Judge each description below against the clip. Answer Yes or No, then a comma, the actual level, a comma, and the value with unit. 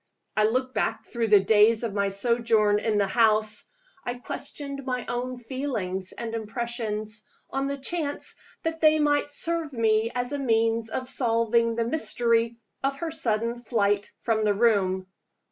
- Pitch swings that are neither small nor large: Yes, average, 3.2 semitones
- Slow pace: No, average, 160 wpm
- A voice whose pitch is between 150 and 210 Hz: No, high, 230 Hz